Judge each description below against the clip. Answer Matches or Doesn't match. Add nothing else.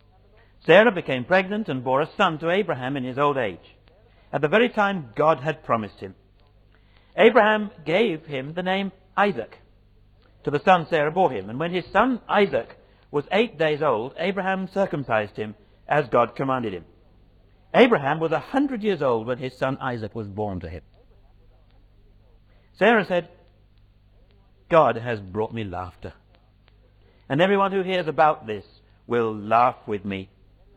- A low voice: Matches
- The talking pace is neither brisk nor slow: Matches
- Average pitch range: Doesn't match